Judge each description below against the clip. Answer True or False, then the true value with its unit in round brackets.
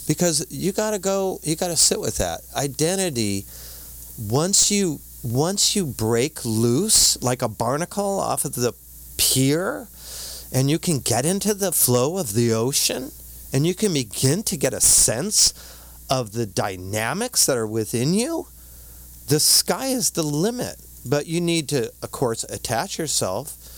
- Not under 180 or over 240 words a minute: False (160 wpm)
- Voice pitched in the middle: False (130 Hz)